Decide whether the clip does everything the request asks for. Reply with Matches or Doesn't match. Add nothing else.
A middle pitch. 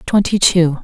Matches